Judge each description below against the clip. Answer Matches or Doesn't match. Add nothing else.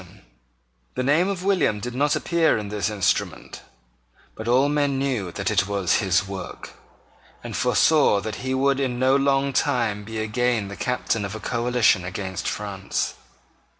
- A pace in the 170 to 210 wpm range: Doesn't match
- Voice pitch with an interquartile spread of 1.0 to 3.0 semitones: Doesn't match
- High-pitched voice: Doesn't match